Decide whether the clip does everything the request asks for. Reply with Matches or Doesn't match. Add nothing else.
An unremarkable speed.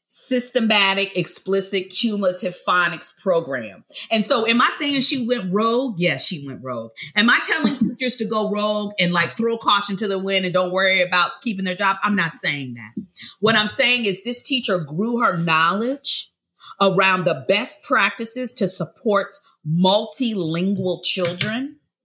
Matches